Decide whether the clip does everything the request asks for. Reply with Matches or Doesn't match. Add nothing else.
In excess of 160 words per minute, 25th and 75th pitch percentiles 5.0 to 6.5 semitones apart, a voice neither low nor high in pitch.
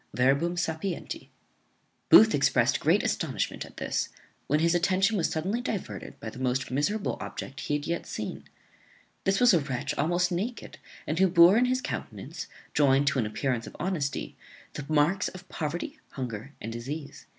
Matches